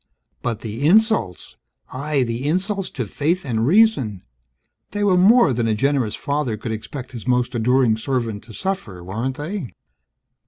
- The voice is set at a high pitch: No, low, 130 Hz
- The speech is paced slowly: No, average, 155 wpm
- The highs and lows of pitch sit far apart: Yes, wide, 7.3 semitones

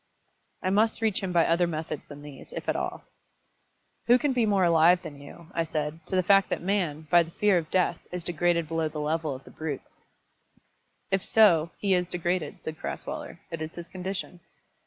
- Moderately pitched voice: Yes, medium, 170 Hz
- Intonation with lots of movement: No, average, 3.0 semitones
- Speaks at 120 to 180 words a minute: No, average, 200 wpm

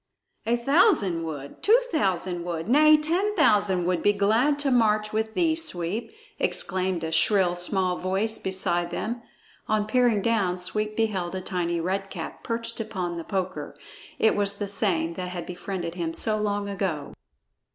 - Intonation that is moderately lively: Yes, average, 3.9 semitones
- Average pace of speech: Yes, average, 160 wpm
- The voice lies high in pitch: Yes, high, 200 Hz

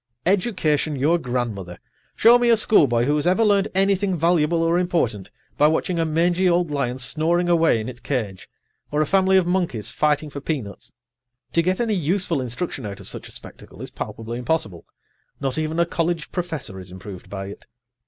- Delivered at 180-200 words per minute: Yes, average, 185 wpm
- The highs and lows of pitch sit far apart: Yes, wide, 6.2 semitones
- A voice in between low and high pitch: Yes, medium, 160 Hz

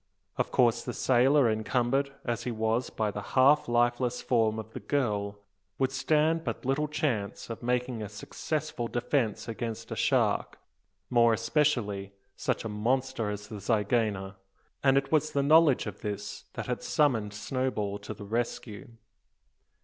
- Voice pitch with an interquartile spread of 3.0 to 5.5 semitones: Yes, average, 3.9 semitones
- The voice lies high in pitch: No, low, 120 Hz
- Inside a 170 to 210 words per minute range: No, average, 155 wpm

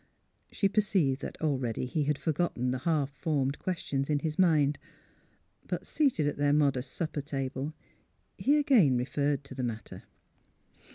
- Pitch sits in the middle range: Yes, medium, 145 Hz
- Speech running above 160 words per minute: No, average, 150 wpm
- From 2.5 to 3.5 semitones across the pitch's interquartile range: Yes, average, 3.2 semitones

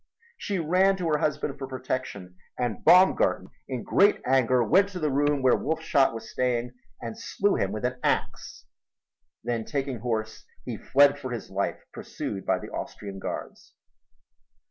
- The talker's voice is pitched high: No, low, 130 Hz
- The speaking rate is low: No, average, 160 wpm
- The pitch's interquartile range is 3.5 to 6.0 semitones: Yes, average, 4.7 semitones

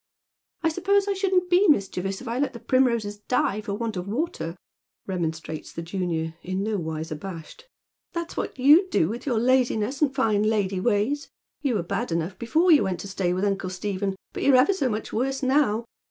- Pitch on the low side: No, high, 215 Hz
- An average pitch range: No, wide, 6.4 semitones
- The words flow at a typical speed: No, fast, 210 wpm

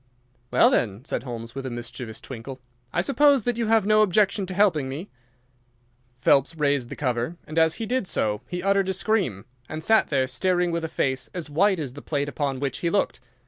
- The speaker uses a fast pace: Yes, fast, 210 wpm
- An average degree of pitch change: No, wide, 6.9 semitones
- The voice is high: No, medium, 155 Hz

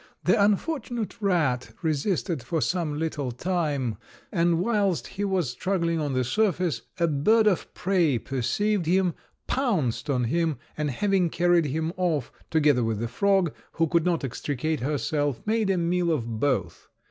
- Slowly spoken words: No, average, 155 wpm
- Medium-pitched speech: Yes, medium, 165 Hz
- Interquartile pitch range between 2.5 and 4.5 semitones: No, average, 5.0 semitones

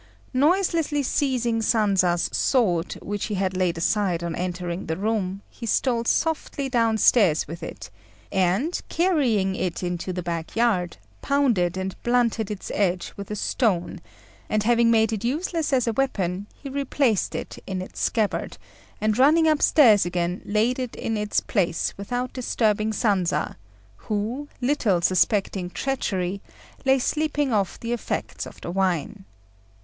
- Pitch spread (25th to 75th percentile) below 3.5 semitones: No, average, 5.3 semitones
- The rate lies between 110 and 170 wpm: Yes, average, 145 wpm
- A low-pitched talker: No, high, 215 Hz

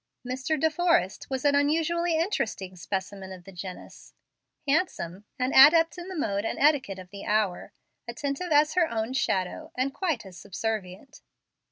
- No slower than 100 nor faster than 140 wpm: No, average, 160 wpm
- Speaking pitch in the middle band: No, very high, 255 Hz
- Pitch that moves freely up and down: Yes, wide, 8.3 semitones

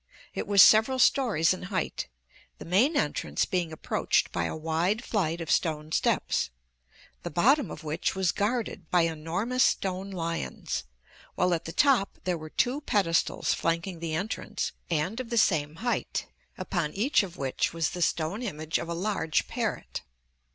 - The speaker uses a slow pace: No, average, 165 wpm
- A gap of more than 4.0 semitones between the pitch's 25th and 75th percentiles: Yes, average, 4.7 semitones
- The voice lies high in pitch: No, medium, 180 Hz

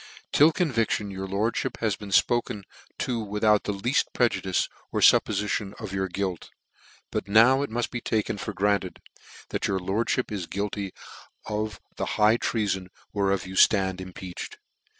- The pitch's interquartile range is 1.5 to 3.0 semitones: Yes, average, 2.7 semitones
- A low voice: Yes, low, 105 Hz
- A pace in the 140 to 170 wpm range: Yes, average, 160 wpm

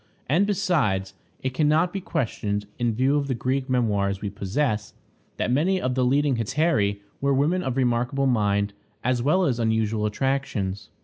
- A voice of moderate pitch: No, low, 125 Hz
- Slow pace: No, average, 170 wpm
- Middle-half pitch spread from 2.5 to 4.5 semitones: No, average, 5.3 semitones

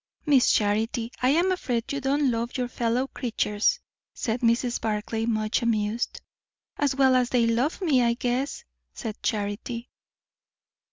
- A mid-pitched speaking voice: No, high, 240 Hz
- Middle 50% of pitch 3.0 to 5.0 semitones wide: No, narrow, 2.6 semitones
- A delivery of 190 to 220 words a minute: No, average, 150 wpm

